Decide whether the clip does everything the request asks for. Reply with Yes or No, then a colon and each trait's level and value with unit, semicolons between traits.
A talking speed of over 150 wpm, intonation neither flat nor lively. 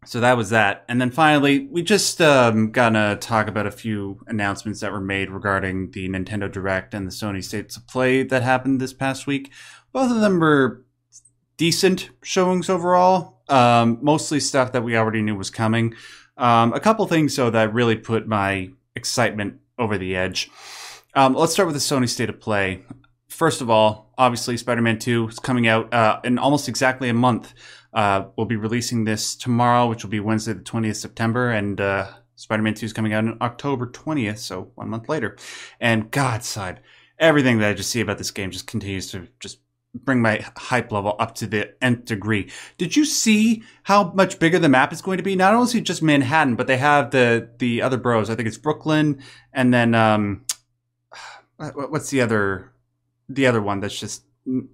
Yes: average, 195 wpm; average, 4.2 semitones